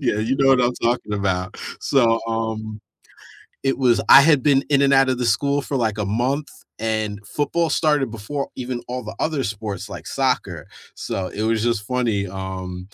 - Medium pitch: No, low, 120 Hz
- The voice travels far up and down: No, average, 4.1 semitones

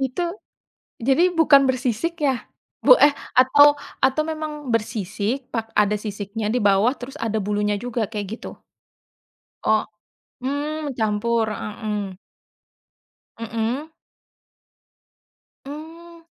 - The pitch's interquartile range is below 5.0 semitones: No, wide, 5.4 semitones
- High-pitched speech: Yes, high, 245 Hz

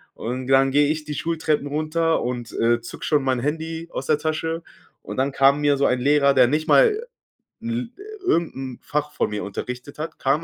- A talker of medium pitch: Yes, medium, 145 Hz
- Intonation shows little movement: No, average, 3.2 semitones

